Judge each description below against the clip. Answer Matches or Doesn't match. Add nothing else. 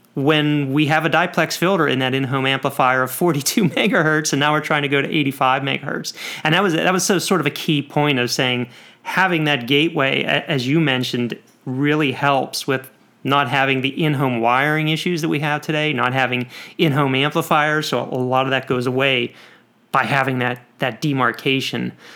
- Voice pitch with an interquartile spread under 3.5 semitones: Matches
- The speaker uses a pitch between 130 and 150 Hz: Matches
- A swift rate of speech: Doesn't match